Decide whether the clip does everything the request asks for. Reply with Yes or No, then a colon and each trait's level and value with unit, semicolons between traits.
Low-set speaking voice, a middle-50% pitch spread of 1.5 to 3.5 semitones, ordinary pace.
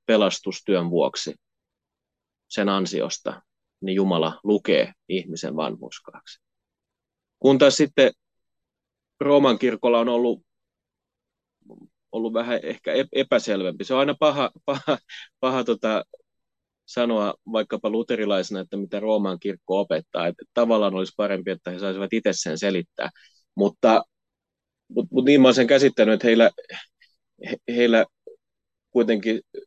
No: low, 115 Hz; average, 5.1 semitones; average, 115 wpm